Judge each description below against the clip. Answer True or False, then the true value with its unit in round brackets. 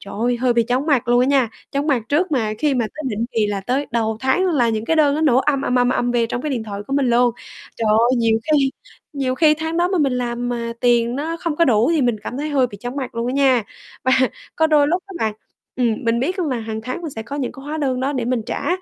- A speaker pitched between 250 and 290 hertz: True (255 Hz)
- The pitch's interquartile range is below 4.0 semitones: True (3.6 semitones)